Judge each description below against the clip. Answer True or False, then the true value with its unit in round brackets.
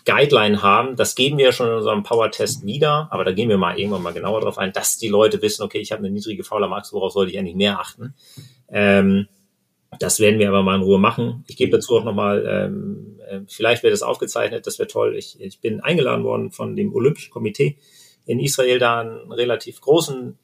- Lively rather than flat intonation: True (6.5 semitones)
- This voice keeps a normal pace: False (225 wpm)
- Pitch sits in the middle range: False (115 Hz)